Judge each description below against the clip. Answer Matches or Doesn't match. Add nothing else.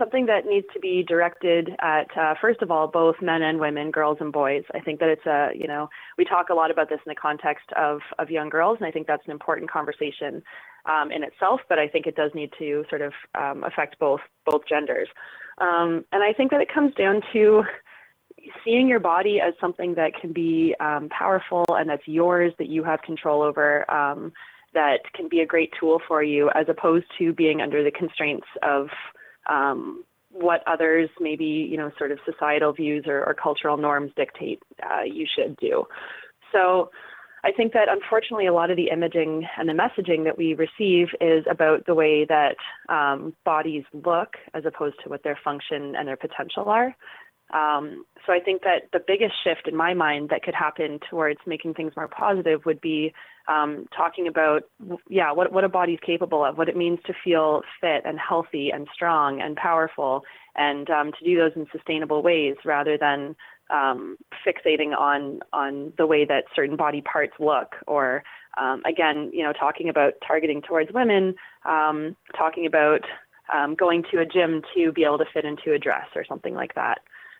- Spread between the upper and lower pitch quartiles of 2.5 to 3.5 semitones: Matches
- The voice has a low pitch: Doesn't match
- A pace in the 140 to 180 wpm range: Doesn't match